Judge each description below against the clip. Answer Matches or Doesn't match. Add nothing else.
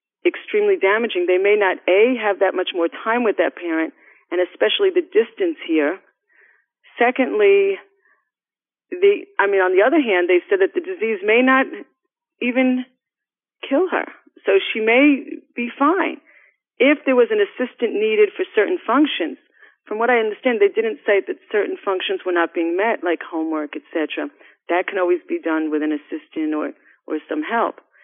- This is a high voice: Matches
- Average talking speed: Matches